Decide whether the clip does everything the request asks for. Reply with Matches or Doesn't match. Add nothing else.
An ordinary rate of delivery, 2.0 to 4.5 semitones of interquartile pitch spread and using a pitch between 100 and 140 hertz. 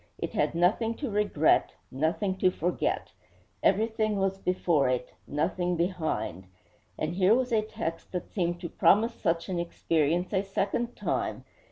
Doesn't match